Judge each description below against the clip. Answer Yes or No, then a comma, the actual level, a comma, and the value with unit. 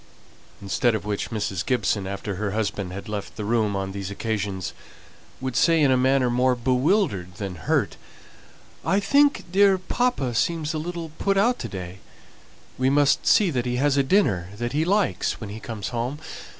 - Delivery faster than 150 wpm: Yes, average, 180 wpm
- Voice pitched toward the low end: Yes, low, 125 Hz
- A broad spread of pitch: Yes, wide, 7.7 semitones